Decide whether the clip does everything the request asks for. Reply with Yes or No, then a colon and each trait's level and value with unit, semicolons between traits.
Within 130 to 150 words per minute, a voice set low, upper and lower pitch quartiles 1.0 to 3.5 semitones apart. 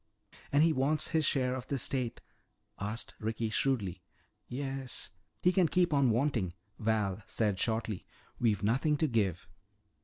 No: average, 145 wpm; low, 120 Hz; average, 4.4 semitones